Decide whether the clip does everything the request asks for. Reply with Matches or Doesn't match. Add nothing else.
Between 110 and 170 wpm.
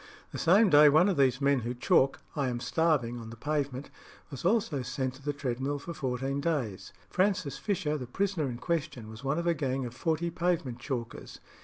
Doesn't match